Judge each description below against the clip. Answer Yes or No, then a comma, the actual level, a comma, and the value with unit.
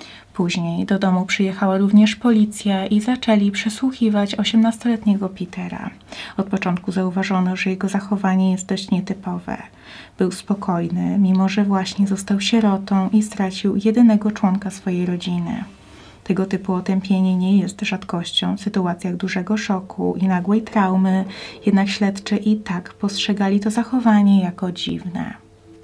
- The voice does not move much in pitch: Yes, narrow, 1.9 semitones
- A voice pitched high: Yes, high, 195 Hz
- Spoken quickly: No, average, 130 wpm